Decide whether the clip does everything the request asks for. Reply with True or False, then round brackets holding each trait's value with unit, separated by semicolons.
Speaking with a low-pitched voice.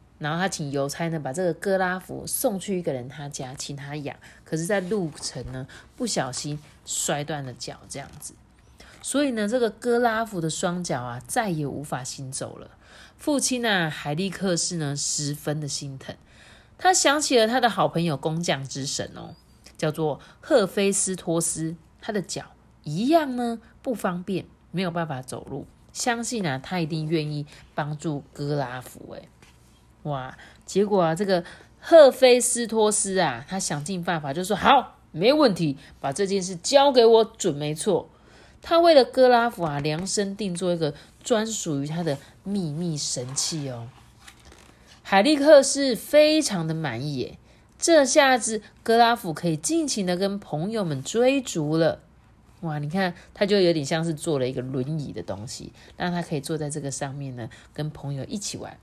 False (170 Hz)